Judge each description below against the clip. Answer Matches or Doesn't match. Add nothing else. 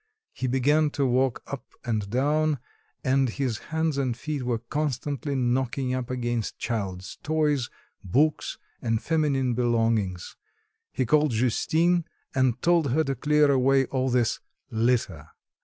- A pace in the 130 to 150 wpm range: Matches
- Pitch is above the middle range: Doesn't match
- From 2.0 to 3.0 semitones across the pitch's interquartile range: Doesn't match